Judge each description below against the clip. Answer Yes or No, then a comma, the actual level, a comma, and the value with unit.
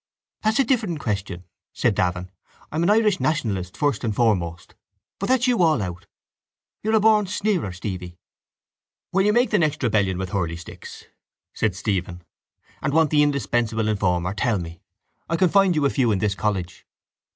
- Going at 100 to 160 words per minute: No, average, 170 wpm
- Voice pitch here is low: Yes, low, 115 Hz